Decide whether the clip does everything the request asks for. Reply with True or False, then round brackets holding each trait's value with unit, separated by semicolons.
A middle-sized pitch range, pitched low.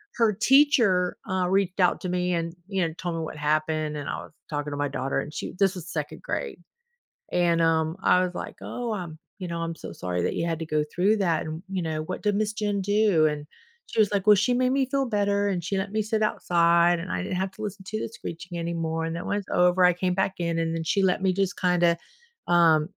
False (3.5 semitones; 180 Hz)